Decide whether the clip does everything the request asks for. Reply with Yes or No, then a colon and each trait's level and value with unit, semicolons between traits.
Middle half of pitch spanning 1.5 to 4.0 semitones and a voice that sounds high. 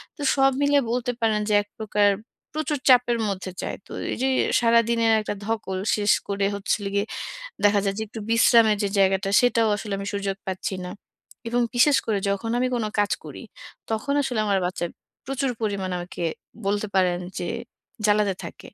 Yes: average, 3.0 semitones; high, 210 Hz